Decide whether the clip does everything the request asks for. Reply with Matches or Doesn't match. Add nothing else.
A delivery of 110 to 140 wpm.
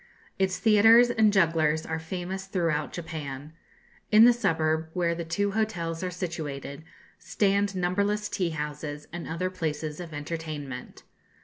Matches